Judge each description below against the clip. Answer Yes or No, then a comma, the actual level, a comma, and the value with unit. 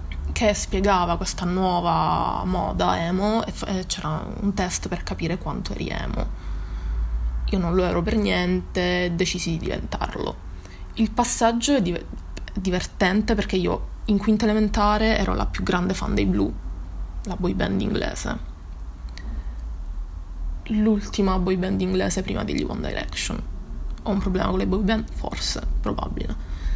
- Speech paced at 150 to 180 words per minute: No, average, 135 wpm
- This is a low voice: No, medium, 180 Hz